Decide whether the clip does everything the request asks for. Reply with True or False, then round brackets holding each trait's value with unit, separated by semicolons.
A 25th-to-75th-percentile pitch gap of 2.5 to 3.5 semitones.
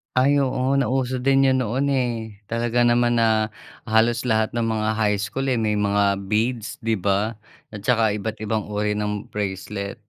True (2.8 semitones)